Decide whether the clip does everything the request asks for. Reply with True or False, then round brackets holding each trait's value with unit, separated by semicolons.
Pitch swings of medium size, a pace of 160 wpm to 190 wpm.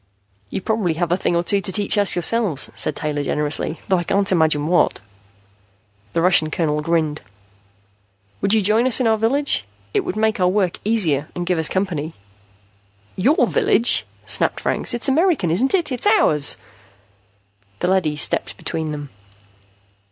False (5.7 semitones; 165 wpm)